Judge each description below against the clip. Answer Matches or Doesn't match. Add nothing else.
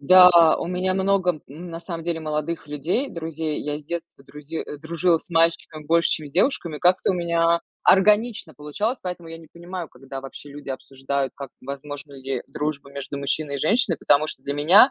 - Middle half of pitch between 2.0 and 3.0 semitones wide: Doesn't match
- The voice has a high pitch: Doesn't match